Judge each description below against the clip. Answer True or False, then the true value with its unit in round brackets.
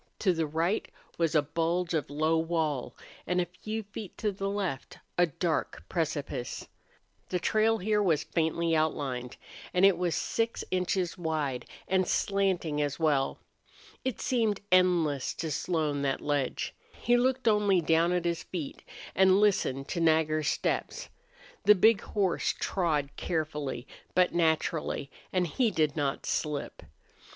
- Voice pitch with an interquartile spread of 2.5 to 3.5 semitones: False (3.9 semitones)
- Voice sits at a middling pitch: True (170 Hz)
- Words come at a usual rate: True (145 wpm)